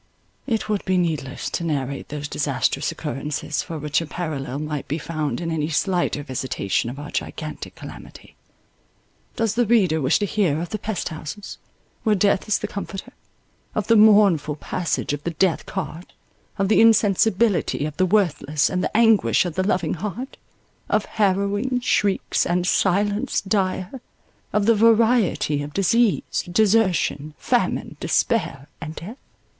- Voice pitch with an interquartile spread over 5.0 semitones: Yes, wide, 5.6 semitones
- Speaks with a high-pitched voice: No, medium, 180 Hz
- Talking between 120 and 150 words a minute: Yes, average, 145 wpm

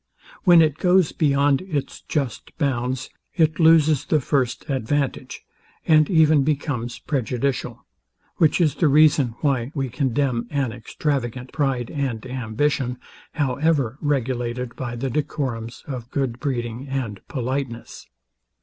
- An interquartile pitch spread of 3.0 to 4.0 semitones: Yes, average, 3.4 semitones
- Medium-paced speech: No, slow, 120 wpm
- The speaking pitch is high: No, low, 135 Hz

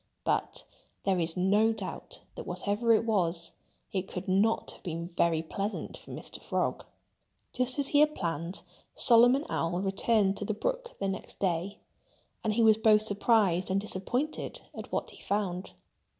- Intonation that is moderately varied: Yes, average, 3.7 semitones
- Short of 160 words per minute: No, average, 165 wpm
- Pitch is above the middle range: Yes, high, 200 Hz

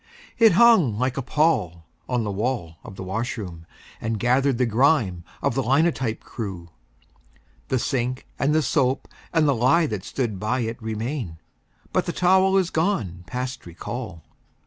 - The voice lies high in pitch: No, low, 125 Hz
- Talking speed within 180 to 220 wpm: No, average, 160 wpm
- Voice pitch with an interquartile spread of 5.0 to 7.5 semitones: Yes, average, 5.3 semitones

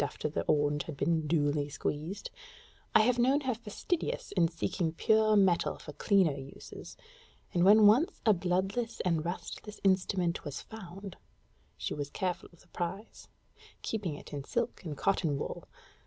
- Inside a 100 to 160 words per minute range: Yes, average, 155 wpm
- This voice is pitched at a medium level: Yes, medium, 180 Hz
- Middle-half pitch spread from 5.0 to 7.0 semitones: Yes, wide, 5.6 semitones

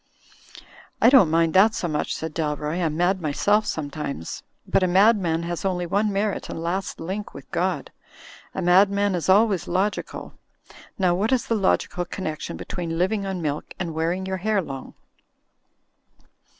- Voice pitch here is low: No, medium, 180 Hz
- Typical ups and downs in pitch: Yes, average, 3.4 semitones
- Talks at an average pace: Yes, average, 160 wpm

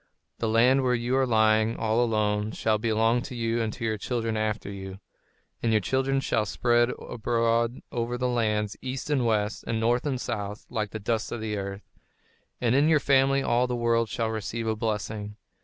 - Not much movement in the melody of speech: Yes, narrow, 2.1 semitones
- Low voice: Yes, low, 115 Hz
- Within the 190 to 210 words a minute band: Yes, average, 195 wpm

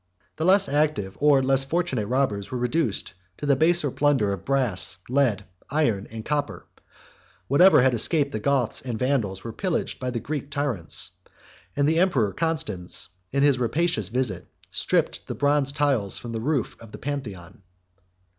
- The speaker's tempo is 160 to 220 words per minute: Yes, average, 165 wpm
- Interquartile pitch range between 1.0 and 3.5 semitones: No, average, 5.0 semitones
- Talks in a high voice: No, low, 135 Hz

